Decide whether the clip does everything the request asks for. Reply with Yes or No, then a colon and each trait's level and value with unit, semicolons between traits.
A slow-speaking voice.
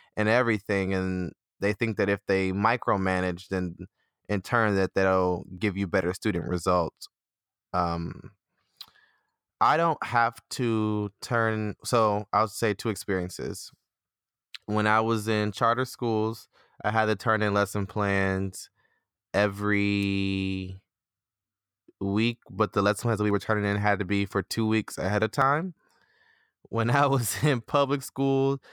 No: average, 145 wpm